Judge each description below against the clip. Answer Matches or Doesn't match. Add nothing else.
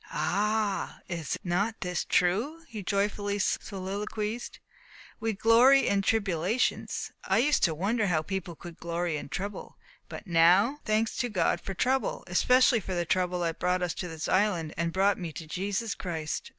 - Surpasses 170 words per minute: Doesn't match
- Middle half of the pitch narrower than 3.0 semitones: Doesn't match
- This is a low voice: Doesn't match